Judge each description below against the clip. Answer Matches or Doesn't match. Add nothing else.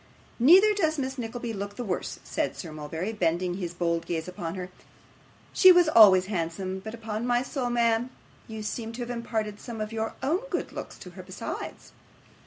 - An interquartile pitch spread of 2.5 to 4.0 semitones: Doesn't match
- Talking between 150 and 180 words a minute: Doesn't match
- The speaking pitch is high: Matches